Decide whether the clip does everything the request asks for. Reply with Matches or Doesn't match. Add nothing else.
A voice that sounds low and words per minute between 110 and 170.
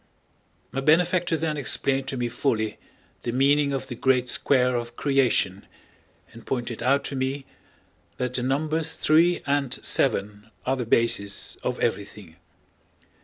Matches